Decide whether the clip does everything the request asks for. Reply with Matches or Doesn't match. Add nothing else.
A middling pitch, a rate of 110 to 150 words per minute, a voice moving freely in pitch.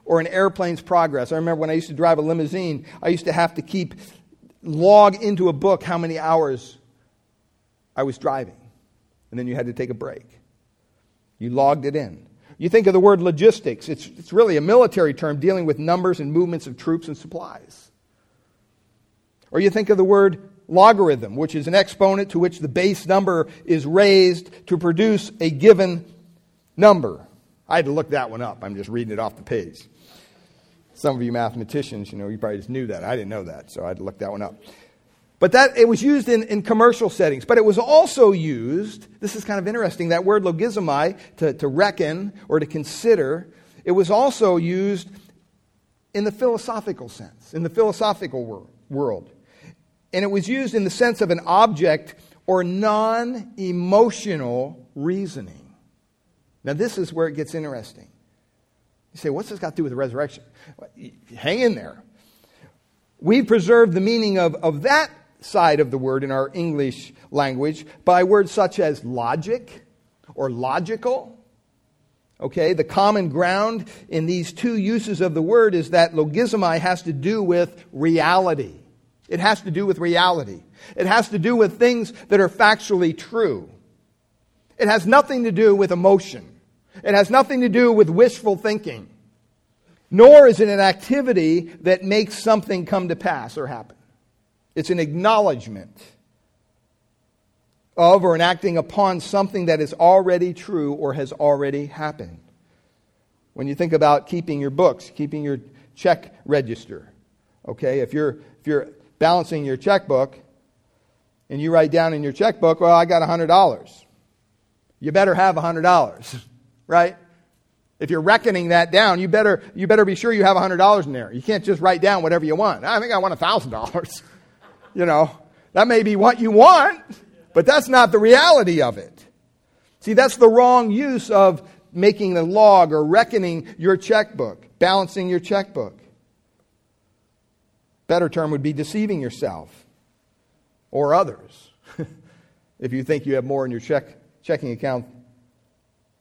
Doesn't match